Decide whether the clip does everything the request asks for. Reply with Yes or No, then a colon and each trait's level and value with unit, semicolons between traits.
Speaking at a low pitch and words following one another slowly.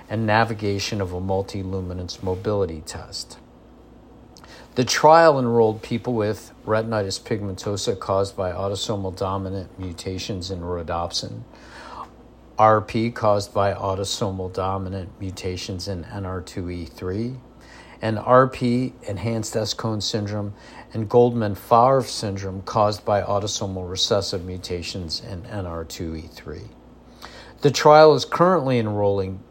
Yes: low, 100 Hz; slow, 100 wpm